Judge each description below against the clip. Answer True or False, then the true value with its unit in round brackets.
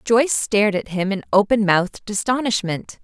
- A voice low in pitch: False (210 Hz)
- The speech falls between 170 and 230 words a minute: False (160 wpm)